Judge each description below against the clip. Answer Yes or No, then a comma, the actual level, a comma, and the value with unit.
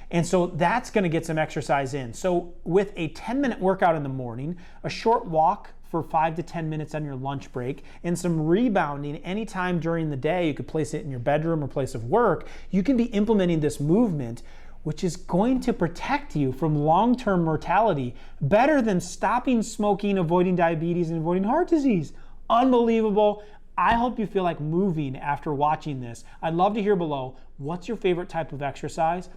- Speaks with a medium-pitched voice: Yes, medium, 170 Hz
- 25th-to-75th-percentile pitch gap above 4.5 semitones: Yes, average, 5.1 semitones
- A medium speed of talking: Yes, average, 190 wpm